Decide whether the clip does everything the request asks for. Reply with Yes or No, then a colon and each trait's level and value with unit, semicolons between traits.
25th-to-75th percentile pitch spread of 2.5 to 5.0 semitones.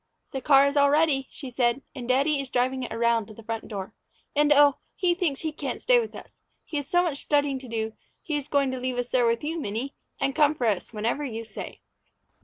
Yes: average, 3.7 semitones